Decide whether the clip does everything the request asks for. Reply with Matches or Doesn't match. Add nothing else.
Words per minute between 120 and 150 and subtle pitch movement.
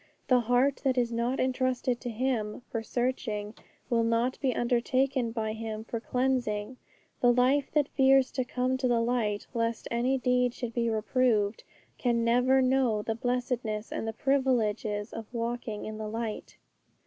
Doesn't match